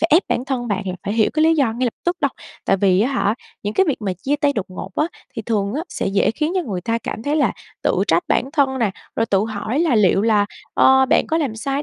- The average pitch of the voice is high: Yes, high, 230 Hz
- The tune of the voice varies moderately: No, wide, 5.8 semitones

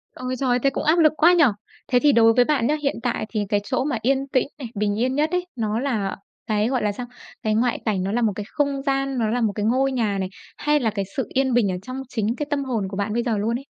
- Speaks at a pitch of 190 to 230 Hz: No, high, 245 Hz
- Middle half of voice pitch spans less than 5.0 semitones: Yes, average, 4.1 semitones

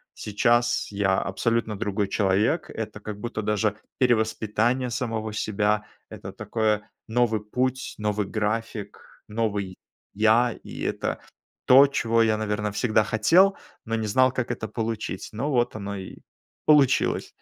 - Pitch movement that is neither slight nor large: No, narrow, 2.3 semitones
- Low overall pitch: Yes, low, 110 Hz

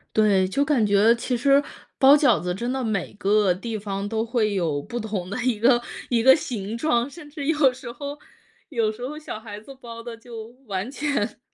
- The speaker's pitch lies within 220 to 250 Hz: Yes, high, 230 Hz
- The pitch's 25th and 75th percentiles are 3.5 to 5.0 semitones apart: Yes, average, 4.1 semitones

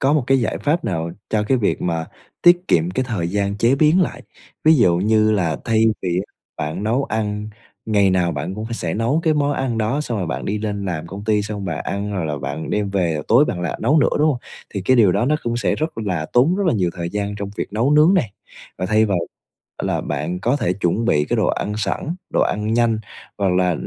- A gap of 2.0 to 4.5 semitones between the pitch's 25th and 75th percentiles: No, average, 5.1 semitones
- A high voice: No, low, 105 Hz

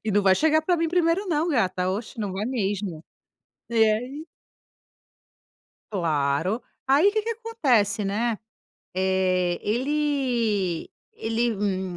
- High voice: Yes, high, 220 Hz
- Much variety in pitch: Yes, wide, 7.7 semitones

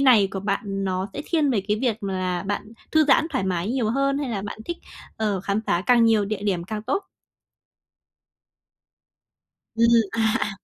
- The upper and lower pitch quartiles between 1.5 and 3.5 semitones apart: No, average, 4.4 semitones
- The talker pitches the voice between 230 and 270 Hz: No, high, 215 Hz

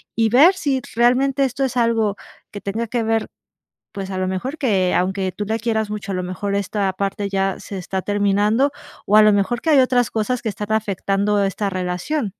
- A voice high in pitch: Yes, high, 210 Hz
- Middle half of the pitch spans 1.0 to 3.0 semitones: No, average, 3.4 semitones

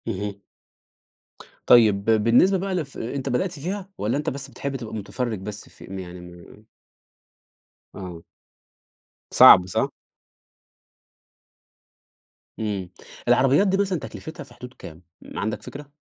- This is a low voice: Yes, low, 120 Hz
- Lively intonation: Yes, wide, 6.4 semitones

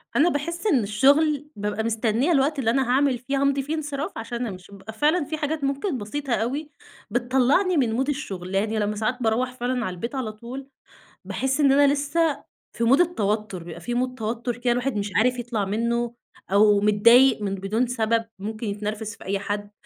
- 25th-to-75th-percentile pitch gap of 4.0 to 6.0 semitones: Yes, average, 4.5 semitones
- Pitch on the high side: Yes, high, 240 Hz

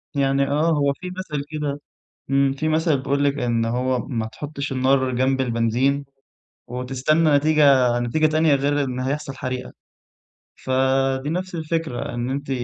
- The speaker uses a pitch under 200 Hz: Yes, medium, 140 Hz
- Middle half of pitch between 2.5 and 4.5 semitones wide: Yes, average, 2.8 semitones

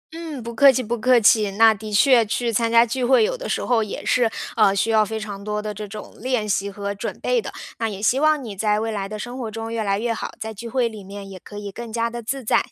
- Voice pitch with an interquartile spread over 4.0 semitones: No, narrow, 2.4 semitones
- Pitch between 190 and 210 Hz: No, high, 225 Hz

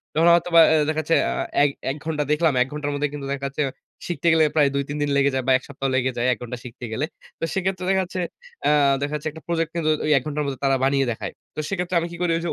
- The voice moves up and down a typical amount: Yes, average, 3.4 semitones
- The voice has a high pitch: No, medium, 150 Hz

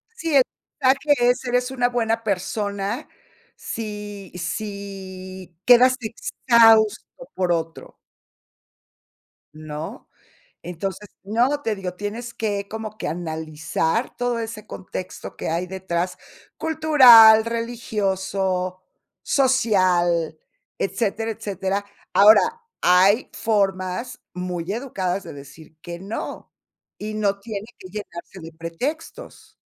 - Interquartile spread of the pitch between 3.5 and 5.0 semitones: Yes, average, 4.1 semitones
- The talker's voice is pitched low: No, high, 200 Hz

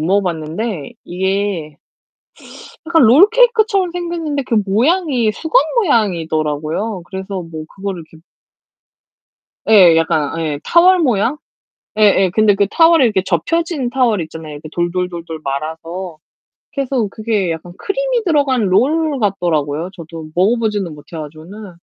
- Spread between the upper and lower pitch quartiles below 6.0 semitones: No, wide, 8.5 semitones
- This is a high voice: Yes, high, 200 Hz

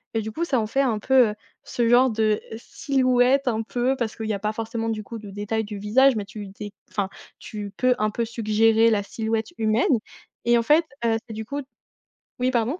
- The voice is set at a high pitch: Yes, high, 225 Hz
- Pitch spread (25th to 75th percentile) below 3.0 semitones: Yes, narrow, 2.6 semitones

